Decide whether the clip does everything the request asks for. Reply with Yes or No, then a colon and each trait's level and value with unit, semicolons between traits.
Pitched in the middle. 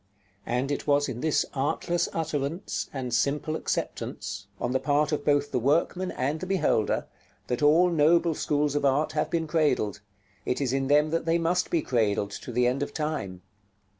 Yes: medium, 145 Hz